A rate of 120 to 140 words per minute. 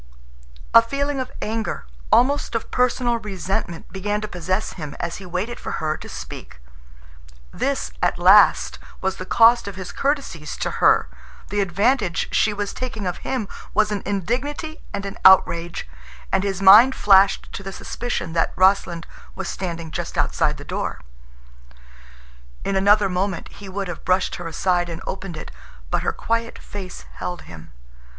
No: average, 160 wpm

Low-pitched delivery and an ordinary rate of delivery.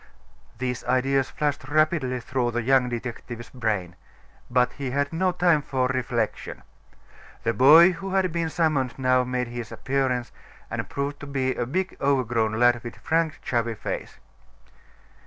Yes: low, 130 Hz; average, 150 wpm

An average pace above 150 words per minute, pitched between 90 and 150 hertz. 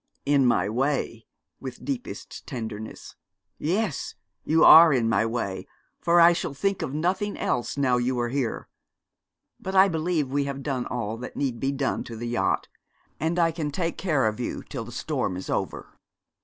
Yes: average, 180 wpm; low, 135 Hz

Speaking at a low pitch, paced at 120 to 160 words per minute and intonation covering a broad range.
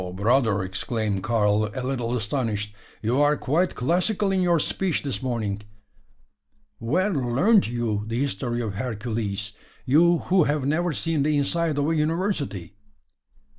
Yes: low, 130 Hz; average, 140 wpm; wide, 6.7 semitones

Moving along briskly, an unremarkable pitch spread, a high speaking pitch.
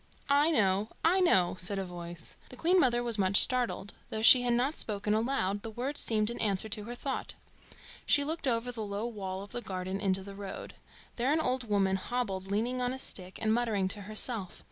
Yes: fast, 210 wpm; average, 4.1 semitones; high, 220 Hz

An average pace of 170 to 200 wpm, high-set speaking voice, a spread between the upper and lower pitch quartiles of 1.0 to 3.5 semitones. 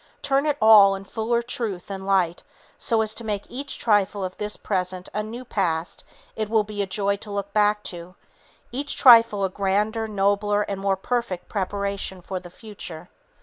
Yes: average, 180 wpm; high, 205 Hz; narrow, 2.4 semitones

